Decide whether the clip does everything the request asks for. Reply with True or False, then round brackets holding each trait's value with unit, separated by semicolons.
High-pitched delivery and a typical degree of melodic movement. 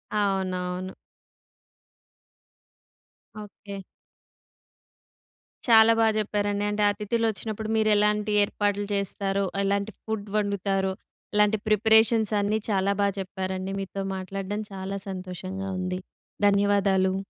False (200 Hz; 1.6 semitones)